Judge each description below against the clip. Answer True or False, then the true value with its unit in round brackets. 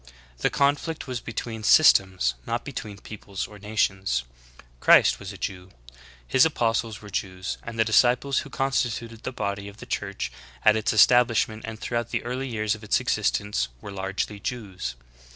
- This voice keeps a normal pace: True (165 wpm)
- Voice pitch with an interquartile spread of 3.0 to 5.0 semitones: True (3.3 semitones)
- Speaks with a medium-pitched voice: False (110 Hz)